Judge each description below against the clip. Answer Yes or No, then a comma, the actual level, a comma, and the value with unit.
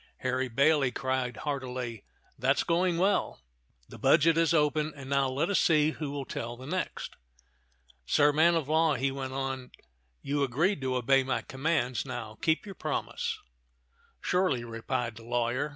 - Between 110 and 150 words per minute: No, average, 160 wpm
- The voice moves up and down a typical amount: Yes, average, 3.7 semitones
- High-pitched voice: No, low, 135 Hz